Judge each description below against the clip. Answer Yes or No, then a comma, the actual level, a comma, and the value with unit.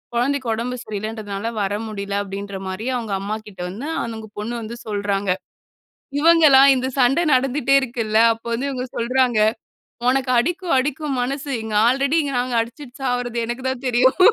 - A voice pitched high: Yes, high, 240 Hz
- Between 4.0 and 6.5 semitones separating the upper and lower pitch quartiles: No, average, 3.5 semitones